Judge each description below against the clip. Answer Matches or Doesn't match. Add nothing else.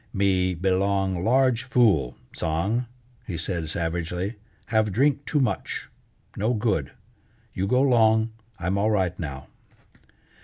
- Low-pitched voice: Matches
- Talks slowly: Matches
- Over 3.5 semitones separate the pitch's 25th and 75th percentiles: Matches